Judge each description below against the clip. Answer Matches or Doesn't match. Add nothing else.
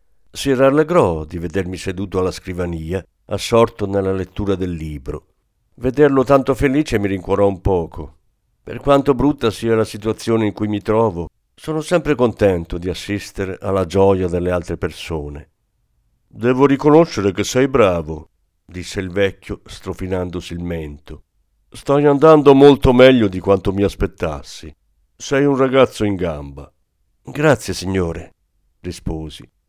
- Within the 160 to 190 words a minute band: Doesn't match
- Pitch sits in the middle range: Doesn't match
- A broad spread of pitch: Matches